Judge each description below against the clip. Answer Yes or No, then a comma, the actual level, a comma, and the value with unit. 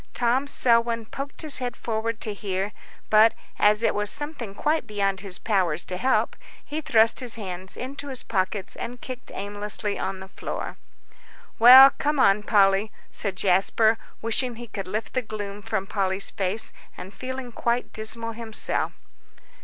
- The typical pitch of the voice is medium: No, high, 220 Hz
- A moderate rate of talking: Yes, average, 160 wpm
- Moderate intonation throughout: Yes, average, 3.7 semitones